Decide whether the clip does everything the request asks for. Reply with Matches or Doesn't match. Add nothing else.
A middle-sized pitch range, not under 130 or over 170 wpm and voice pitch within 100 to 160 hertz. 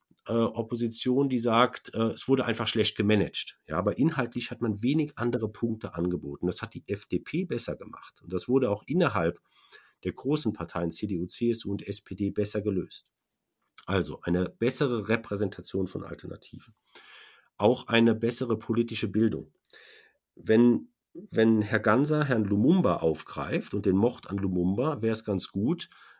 Matches